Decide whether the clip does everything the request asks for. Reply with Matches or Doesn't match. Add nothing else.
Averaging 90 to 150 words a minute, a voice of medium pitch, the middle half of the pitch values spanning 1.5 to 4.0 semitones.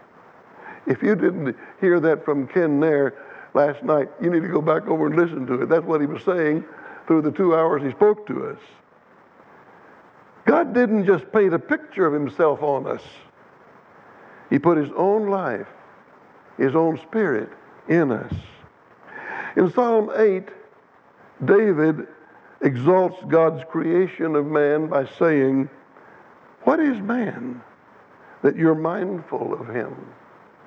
Doesn't match